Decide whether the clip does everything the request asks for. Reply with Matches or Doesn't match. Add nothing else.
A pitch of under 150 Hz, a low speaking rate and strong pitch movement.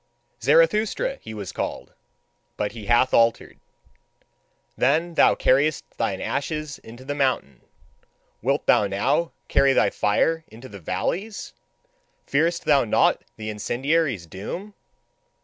Matches